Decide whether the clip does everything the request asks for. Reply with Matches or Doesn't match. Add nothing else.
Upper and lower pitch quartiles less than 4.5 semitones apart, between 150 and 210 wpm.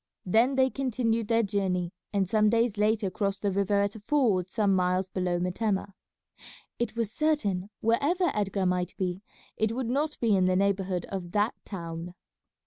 Matches